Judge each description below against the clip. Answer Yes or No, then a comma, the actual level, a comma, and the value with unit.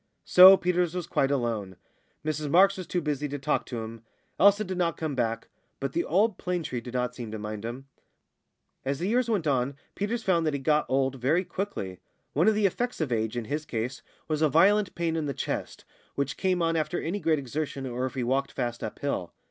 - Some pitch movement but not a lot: No, wide, 6.2 semitones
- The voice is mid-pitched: Yes, medium, 150 Hz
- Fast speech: Yes, fast, 220 wpm